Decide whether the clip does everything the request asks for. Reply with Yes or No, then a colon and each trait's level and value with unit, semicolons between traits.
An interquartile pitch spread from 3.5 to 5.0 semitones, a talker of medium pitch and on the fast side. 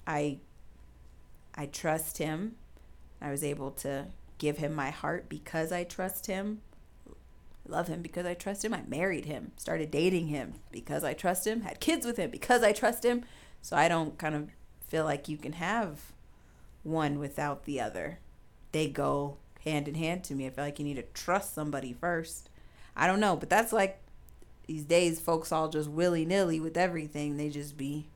No: average, 3.8 semitones; medium, 155 Hz; average, 185 wpm